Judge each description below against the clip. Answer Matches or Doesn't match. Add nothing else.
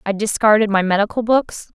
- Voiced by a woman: Matches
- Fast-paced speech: Doesn't match